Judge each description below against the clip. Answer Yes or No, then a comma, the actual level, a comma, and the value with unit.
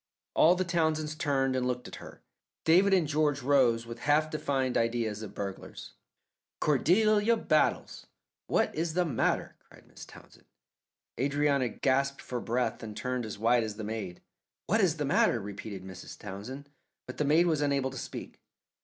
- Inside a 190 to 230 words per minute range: No, average, 170 wpm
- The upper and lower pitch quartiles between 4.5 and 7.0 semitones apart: Yes, average, 5.1 semitones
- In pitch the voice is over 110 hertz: Yes, low, 135 Hz